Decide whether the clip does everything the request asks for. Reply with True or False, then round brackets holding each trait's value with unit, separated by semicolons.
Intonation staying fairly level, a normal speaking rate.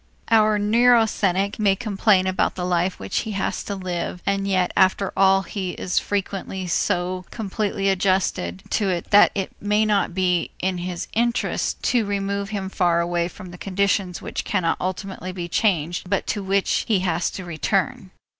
True (2.1 semitones; 170 wpm)